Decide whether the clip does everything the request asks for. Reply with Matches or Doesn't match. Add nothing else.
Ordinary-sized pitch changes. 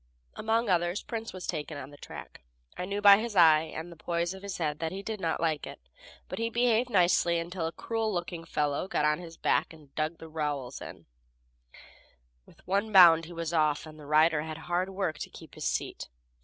Matches